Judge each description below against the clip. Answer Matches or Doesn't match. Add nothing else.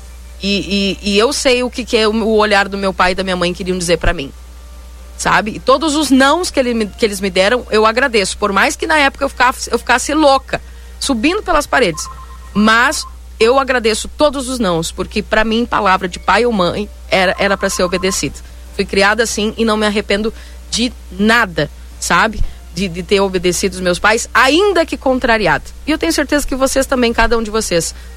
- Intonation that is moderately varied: Doesn't match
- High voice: Matches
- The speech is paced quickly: Matches